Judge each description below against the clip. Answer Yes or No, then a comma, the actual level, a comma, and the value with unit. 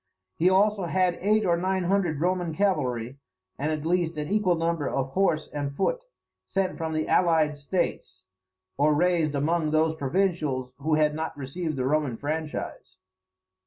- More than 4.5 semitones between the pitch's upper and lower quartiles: No, average, 3.6 semitones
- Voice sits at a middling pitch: Yes, medium, 160 Hz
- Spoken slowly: No, average, 160 wpm